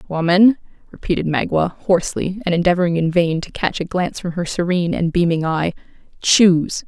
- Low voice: No, medium, 175 Hz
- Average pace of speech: Yes, average, 165 wpm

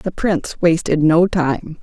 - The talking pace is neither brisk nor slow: Yes, average, 165 wpm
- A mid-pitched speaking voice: Yes, medium, 165 Hz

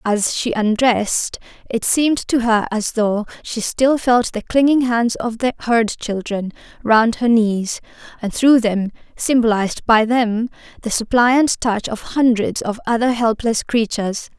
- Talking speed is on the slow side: No, average, 155 wpm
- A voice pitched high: Yes, high, 230 Hz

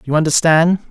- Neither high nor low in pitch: Yes, medium, 165 Hz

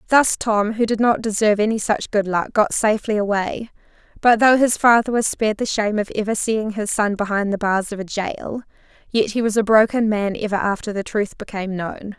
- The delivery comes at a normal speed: No, fast, 215 wpm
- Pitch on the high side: Yes, high, 215 Hz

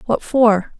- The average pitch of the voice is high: Yes, high, 225 Hz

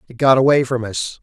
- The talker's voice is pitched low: Yes, low, 125 Hz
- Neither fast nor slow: No, fast, 245 wpm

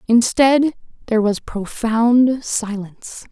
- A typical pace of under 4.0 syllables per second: Yes, 3.7 syllables/s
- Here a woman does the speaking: Yes, female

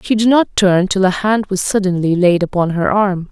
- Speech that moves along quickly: Yes, fast, 235 wpm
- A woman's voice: Yes, female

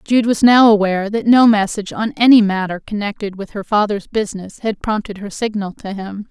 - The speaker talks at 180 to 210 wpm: Yes, average, 200 wpm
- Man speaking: No, female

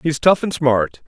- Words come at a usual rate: No, fast, 225 wpm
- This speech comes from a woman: No, male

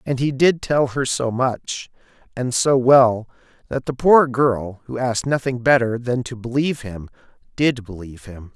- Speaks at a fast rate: No, average, 175 wpm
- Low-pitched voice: Yes, low, 125 Hz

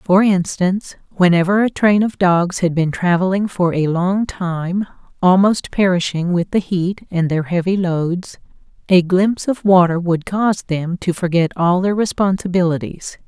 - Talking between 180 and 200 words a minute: No, average, 160 wpm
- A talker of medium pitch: Yes, medium, 180 Hz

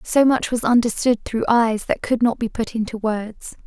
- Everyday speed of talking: No, fast, 215 wpm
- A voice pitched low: No, high, 230 Hz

